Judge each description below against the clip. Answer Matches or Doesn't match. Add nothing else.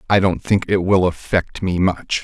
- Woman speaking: Doesn't match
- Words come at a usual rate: Doesn't match